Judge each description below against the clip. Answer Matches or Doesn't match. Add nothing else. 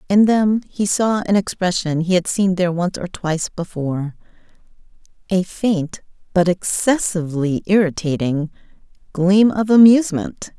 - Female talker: Matches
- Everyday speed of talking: Doesn't match